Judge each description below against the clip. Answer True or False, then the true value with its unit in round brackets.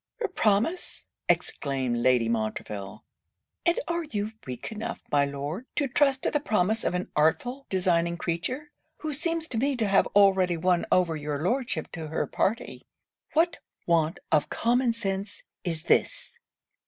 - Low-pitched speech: False (190 Hz)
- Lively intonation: True (8.5 semitones)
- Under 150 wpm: False (155 wpm)